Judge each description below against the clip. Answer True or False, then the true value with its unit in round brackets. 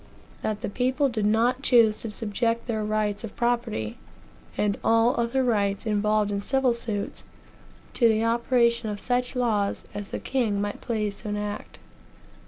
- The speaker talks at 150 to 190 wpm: True (160 wpm)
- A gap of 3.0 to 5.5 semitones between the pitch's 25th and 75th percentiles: False (2.5 semitones)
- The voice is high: True (225 Hz)